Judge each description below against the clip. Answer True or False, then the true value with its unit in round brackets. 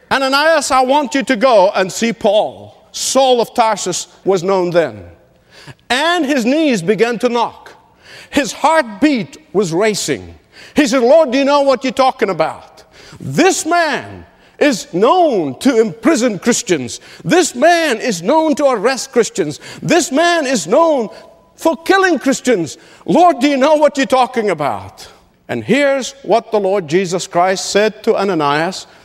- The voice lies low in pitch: False (255 Hz)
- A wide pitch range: True (7.0 semitones)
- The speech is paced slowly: False (155 wpm)